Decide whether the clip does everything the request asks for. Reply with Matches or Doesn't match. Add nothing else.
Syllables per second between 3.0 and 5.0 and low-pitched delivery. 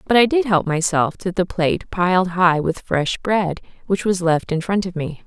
Doesn't match